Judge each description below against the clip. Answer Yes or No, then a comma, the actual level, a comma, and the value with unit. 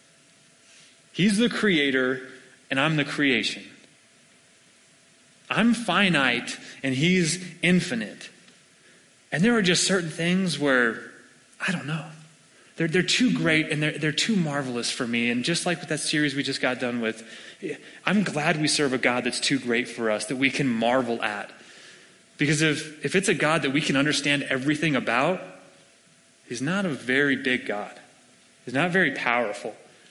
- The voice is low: No, medium, 150 Hz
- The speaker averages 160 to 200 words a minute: Yes, average, 165 wpm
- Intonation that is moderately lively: Yes, average, 4.9 semitones